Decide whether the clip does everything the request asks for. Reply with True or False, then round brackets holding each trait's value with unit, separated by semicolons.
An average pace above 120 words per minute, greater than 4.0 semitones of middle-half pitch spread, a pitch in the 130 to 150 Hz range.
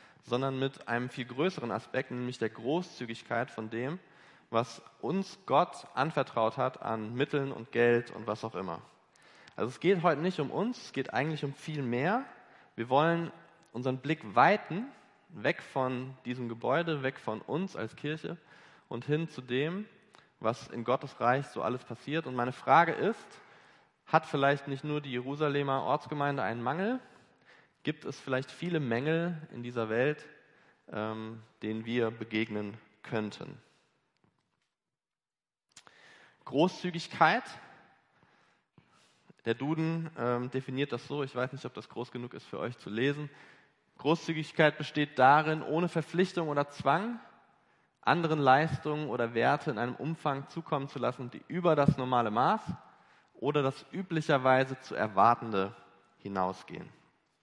True (140 wpm; 4.6 semitones; 135 Hz)